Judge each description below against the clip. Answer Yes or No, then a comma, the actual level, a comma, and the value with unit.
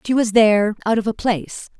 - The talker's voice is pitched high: Yes, high, 215 Hz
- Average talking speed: No, fast, 235 wpm